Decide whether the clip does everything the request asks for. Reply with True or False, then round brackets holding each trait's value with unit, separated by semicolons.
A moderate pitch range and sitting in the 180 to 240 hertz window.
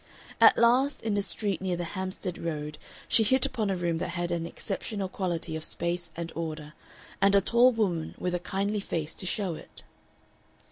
True (3.3 semitones; 185 Hz)